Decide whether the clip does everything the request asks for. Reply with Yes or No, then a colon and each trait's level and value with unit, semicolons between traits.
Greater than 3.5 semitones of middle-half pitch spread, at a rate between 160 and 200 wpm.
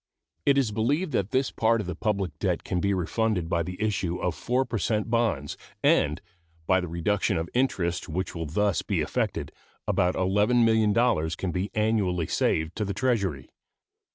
Yes: average, 4.3 semitones; average, 175 wpm